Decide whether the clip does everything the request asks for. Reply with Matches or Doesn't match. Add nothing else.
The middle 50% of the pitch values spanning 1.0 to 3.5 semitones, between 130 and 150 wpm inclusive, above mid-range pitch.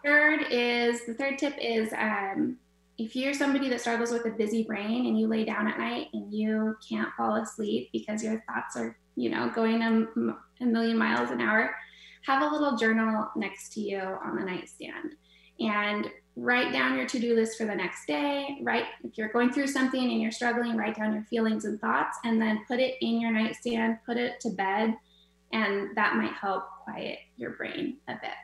Doesn't match